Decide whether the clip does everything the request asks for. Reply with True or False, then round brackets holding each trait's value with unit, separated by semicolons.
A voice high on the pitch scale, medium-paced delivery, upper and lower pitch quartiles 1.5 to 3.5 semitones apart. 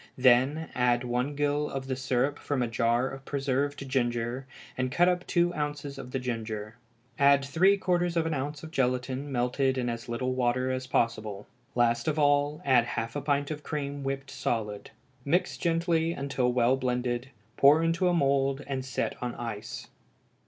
False (135 Hz; 180 wpm; 2.9 semitones)